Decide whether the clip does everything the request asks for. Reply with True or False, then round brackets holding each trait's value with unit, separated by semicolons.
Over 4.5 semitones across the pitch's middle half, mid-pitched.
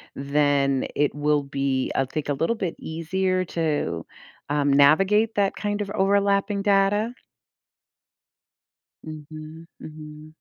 True (5.3 semitones; 155 Hz)